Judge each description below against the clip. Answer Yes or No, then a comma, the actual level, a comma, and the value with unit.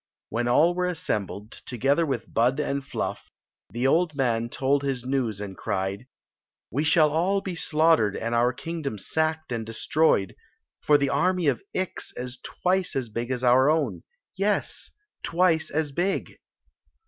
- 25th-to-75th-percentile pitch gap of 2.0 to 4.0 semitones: No, average, 5.2 semitones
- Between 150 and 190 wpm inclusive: Yes, average, 160 wpm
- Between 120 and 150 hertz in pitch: Yes, medium, 140 Hz